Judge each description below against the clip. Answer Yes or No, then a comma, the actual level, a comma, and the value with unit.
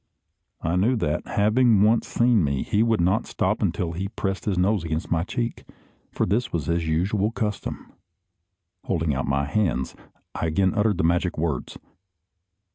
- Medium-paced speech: Yes, average, 170 wpm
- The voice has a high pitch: No, very low, 95 Hz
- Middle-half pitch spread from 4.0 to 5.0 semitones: Yes, average, 4.7 semitones